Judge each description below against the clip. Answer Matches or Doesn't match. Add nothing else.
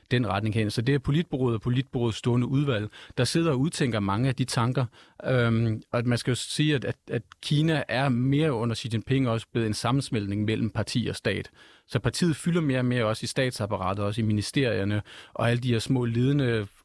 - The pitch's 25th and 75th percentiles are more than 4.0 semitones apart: Doesn't match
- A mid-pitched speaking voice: Doesn't match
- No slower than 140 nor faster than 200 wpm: Doesn't match